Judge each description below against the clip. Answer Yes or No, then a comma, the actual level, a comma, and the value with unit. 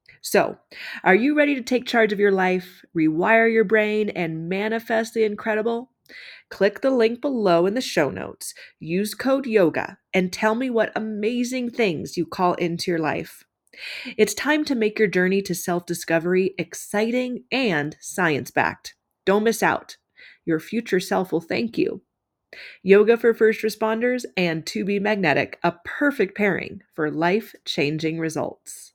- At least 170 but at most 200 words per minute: No, average, 150 wpm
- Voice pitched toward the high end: Yes, high, 215 Hz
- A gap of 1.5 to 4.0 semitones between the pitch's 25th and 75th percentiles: No, average, 4.7 semitones